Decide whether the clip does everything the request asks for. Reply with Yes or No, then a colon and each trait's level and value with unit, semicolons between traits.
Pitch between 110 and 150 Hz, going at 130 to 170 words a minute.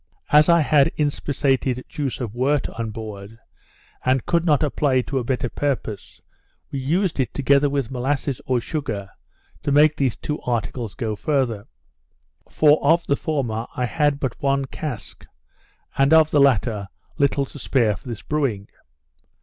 Yes: low, 135 Hz; average, 160 wpm